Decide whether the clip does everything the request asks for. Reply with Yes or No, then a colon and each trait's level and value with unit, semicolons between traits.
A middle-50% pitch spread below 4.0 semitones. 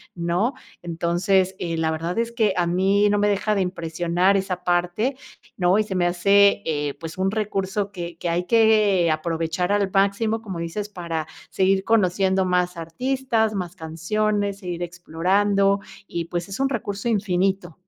Yes: average, 2.9 semitones